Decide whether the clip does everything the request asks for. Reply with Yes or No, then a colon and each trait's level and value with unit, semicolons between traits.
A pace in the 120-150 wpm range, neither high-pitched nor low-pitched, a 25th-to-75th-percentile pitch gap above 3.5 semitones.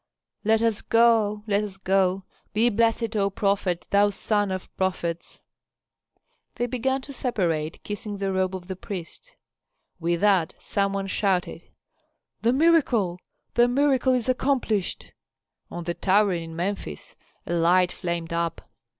No: average, 140 wpm; high, 200 Hz; average, 4.1 semitones